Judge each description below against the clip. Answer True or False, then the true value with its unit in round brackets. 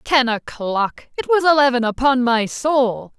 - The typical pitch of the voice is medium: False (255 Hz)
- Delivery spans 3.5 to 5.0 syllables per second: True (3.9 syllables/s)